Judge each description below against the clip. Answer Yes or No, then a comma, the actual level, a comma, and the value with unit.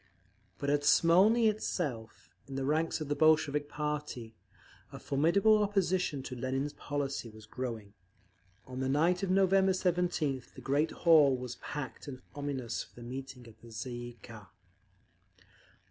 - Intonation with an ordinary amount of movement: Yes, average, 4.7 semitones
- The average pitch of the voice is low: No, medium, 145 Hz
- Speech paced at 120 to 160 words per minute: Yes, average, 150 wpm